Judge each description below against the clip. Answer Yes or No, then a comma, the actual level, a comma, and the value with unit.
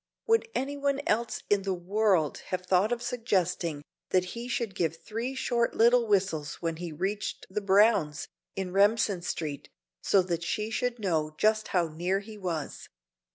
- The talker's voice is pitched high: Yes, high, 195 Hz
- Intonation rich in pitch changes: No, average, 4.7 semitones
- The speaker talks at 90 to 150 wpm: No, average, 165 wpm